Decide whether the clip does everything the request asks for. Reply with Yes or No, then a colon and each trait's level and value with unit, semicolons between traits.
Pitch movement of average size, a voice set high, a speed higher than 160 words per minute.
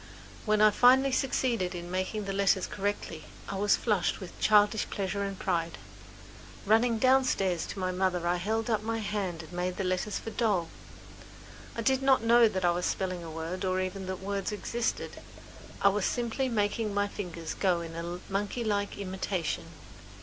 Yes: average, 3.1 semitones; high, 200 Hz; average, 175 wpm